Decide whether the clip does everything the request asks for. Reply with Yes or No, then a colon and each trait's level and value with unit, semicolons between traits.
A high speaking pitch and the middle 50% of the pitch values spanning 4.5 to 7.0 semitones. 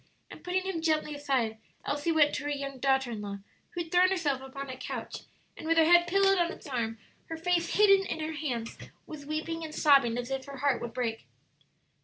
No: very high, 295 Hz; average, 4.0 semitones